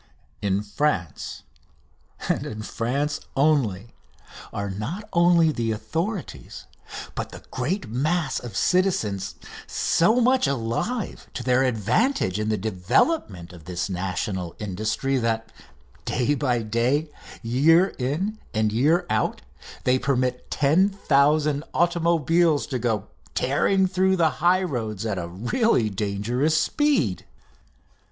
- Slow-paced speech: Yes, slow, 115 wpm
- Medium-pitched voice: No, low, 130 Hz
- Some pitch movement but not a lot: No, wide, 7.6 semitones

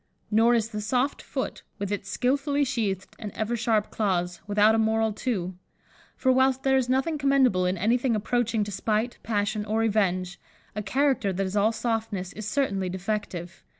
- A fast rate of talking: No, average, 175 wpm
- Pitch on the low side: No, high, 220 Hz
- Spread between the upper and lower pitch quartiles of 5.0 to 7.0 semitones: No, average, 3.7 semitones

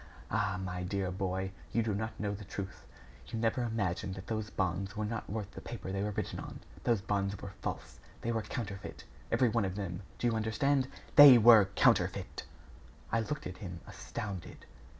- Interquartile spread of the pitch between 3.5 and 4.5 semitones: No, average, 2.9 semitones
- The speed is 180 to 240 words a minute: Yes, average, 190 wpm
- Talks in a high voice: No, low, 105 Hz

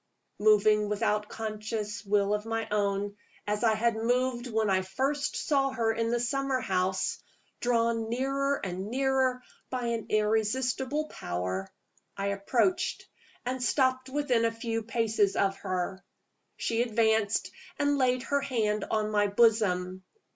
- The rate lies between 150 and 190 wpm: No, average, 140 wpm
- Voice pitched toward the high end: Yes, high, 225 Hz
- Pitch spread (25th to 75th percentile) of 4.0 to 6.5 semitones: No, average, 3.4 semitones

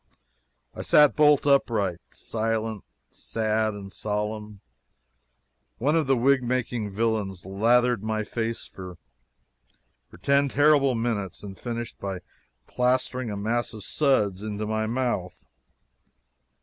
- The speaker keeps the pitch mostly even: No, average, 3.5 semitones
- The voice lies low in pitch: Yes, low, 110 Hz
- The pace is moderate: No, slow, 115 wpm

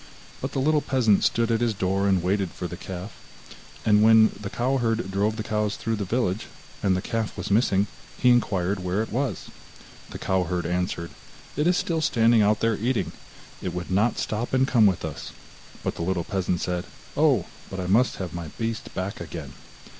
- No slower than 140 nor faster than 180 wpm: No, fast, 205 wpm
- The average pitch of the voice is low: Yes, low, 105 Hz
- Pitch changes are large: No, average, 3.9 semitones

